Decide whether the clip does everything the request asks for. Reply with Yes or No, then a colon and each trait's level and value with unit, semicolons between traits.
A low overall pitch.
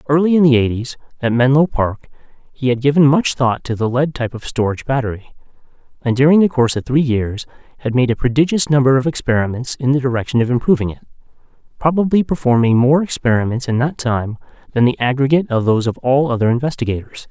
Yes: low, 130 Hz